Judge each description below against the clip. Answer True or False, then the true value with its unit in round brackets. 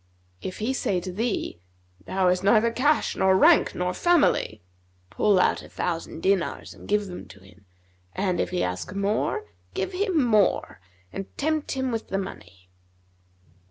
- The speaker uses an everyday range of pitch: True (4.5 semitones)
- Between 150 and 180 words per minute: True (160 wpm)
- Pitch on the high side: True (195 Hz)